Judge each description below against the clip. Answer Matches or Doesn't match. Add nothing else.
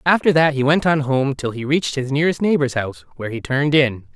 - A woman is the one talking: Doesn't match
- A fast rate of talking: Matches